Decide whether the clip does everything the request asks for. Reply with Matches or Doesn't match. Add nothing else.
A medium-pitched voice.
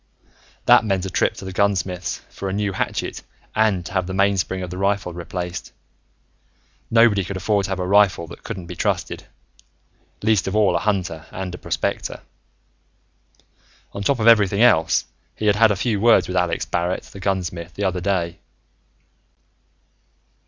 Doesn't match